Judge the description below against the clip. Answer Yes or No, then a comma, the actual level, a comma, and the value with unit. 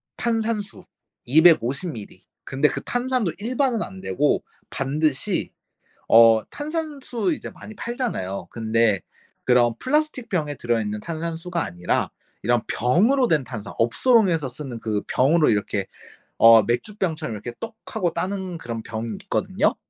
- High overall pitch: No, medium, 155 Hz